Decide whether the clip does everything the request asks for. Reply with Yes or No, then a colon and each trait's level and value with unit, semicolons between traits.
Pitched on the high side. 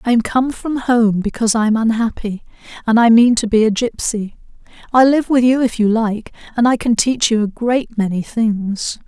Yes: high, 230 Hz